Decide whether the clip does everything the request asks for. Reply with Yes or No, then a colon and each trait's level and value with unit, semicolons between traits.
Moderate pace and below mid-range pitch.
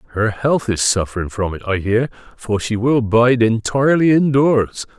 Yes: average, 170 wpm; low, 115 Hz